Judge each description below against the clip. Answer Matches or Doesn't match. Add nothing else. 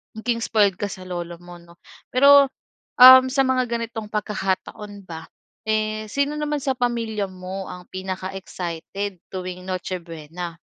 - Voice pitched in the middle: Doesn't match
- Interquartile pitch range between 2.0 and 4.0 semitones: Doesn't match